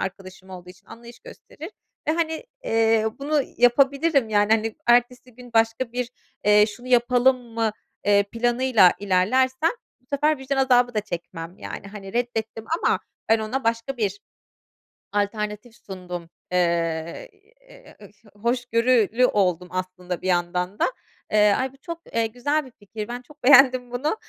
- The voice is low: No, high, 230 Hz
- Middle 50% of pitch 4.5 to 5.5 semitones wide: No, average, 4.1 semitones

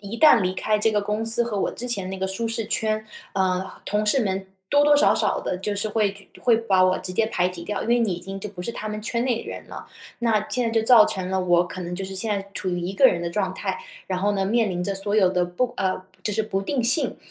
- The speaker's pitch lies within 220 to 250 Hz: No, high, 205 Hz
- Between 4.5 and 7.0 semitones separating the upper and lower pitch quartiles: No, average, 3.2 semitones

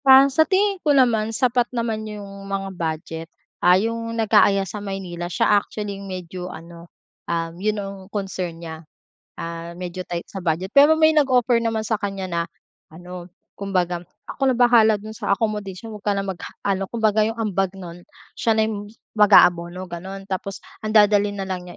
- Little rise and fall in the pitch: No, average, 3.6 semitones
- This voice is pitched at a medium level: No, high, 200 Hz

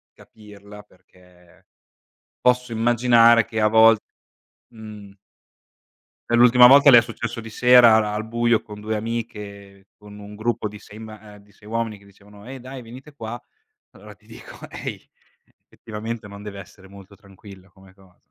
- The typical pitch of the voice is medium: No, low, 110 Hz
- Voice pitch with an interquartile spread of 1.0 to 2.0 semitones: No, narrow, 2.5 semitones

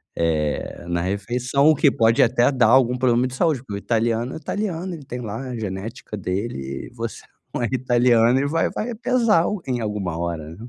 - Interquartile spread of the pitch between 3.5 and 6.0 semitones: Yes, average, 4.7 semitones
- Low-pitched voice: Yes, low, 120 Hz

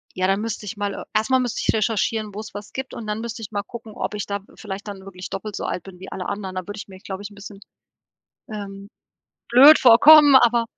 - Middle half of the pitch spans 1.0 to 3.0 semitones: Yes, narrow, 2.5 semitones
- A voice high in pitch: Yes, high, 210 Hz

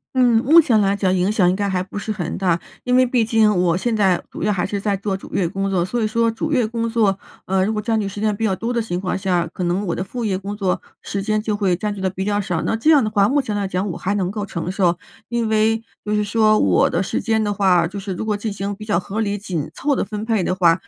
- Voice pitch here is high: Yes, high, 205 Hz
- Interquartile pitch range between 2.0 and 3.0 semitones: Yes, average, 2.7 semitones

